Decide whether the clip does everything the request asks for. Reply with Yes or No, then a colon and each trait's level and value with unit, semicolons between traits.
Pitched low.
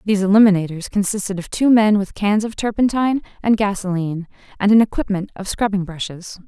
No: high, 200 Hz